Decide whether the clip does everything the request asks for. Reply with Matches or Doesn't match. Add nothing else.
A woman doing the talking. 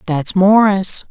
Matches